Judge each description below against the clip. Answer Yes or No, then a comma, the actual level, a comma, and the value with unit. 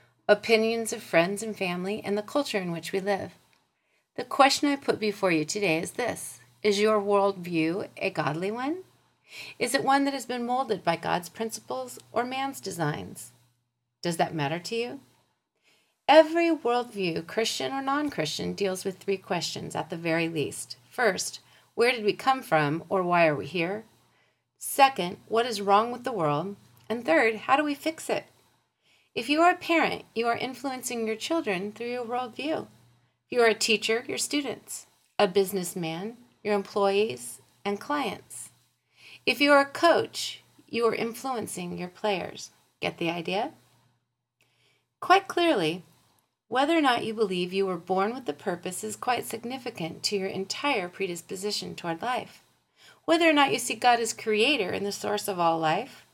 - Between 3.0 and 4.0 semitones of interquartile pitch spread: No, wide, 5.5 semitones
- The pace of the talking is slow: No, average, 170 wpm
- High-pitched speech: Yes, high, 210 Hz